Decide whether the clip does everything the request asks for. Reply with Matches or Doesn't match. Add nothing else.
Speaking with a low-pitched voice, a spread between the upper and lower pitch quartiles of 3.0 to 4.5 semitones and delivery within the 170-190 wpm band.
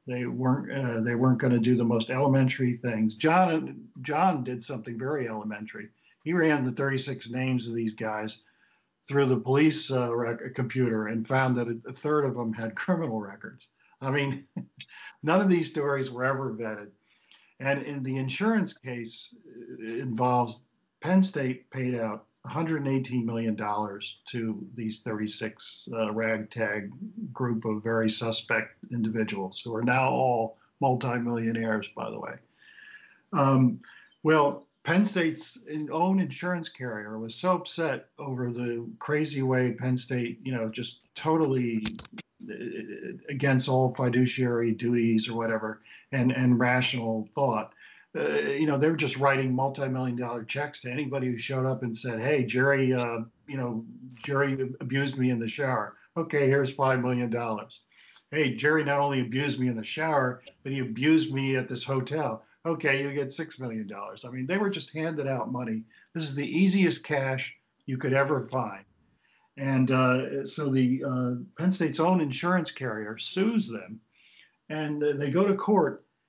Doesn't match